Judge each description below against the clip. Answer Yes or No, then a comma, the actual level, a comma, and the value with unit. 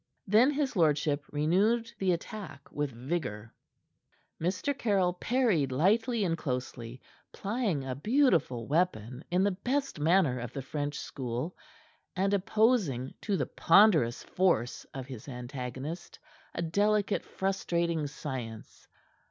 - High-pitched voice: No, medium, 165 Hz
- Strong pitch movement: Yes, wide, 7.3 semitones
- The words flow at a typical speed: No, slow, 120 wpm